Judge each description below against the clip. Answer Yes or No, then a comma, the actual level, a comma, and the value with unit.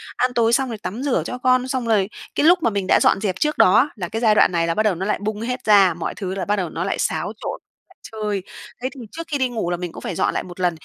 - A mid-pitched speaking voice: No, high, 215 Hz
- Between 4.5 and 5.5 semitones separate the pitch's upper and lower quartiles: Yes, average, 5.1 semitones